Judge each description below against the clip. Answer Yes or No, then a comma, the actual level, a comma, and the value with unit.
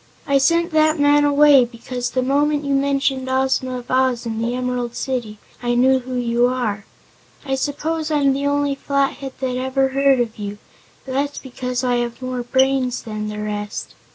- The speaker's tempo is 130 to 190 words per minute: Yes, average, 180 wpm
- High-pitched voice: Yes, very high, 260 Hz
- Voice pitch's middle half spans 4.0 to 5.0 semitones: No, narrow, 2.4 semitones